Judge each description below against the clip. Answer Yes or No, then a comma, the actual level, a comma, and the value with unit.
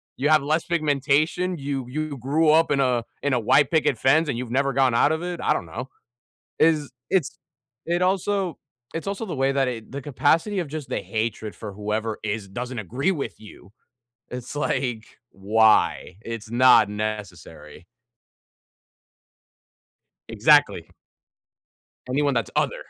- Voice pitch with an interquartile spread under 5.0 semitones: No, wide, 5.6 semitones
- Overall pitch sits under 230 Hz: Yes, low, 135 Hz